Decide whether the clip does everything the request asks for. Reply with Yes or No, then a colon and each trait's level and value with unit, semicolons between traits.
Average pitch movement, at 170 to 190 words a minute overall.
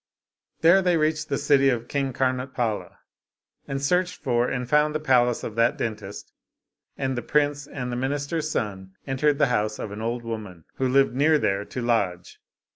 Yes: average, 3.9 semitones; average, 180 wpm